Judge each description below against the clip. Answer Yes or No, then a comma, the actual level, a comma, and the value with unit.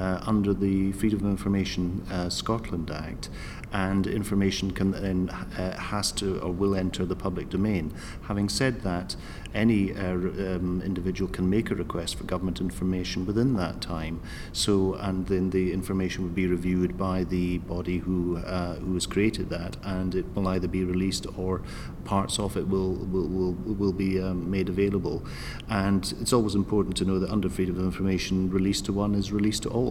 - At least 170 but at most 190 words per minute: Yes, average, 185 wpm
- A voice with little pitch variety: Yes, narrow, 1.5 semitones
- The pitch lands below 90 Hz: No, very low, 95 Hz